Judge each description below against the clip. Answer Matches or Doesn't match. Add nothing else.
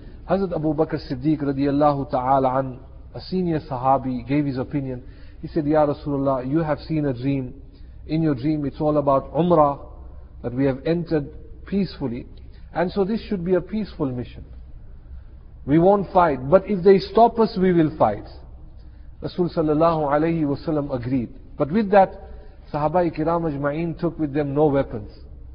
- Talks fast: Doesn't match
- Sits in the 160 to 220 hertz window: Doesn't match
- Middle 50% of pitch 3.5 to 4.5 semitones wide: Matches